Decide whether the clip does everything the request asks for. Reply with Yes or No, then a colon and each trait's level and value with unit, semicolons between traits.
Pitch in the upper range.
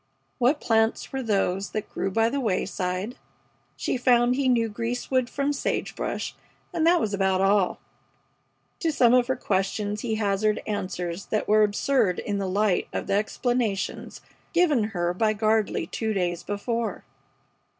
Yes: high, 215 Hz